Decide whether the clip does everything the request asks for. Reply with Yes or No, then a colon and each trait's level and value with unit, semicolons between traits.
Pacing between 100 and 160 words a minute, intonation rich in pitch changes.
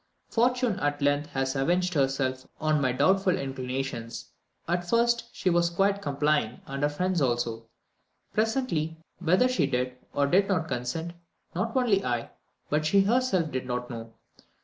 Yes: average, 150 wpm; wide, 6.3 semitones